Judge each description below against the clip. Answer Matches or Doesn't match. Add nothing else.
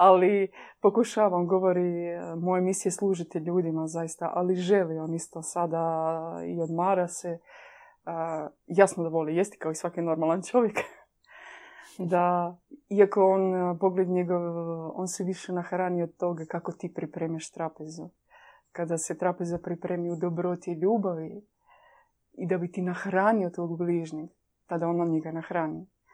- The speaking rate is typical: Matches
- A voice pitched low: Doesn't match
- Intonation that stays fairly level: Matches